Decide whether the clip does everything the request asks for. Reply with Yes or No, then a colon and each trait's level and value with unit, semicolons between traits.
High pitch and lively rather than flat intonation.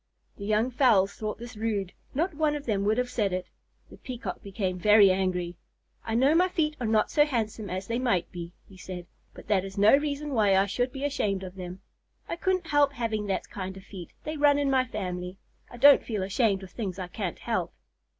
Yes: high, 215 Hz; wide, 5.7 semitones